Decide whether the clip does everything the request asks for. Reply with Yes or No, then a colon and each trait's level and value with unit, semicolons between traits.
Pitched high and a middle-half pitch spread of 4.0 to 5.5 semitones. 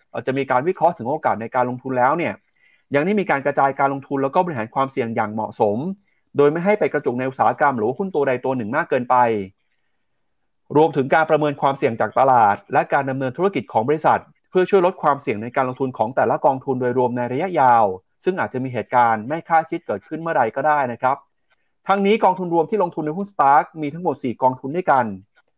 No: medium, 140 Hz; average, 4.4 semitones